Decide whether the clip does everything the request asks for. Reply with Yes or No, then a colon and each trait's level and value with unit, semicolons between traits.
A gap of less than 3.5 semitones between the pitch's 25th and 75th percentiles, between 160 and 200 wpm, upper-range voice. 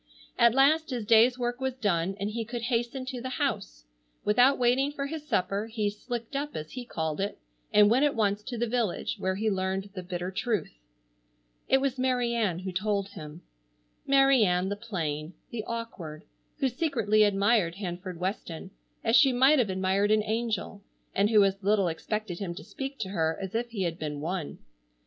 No: average, 4.5 semitones; average, 190 wpm; high, 210 Hz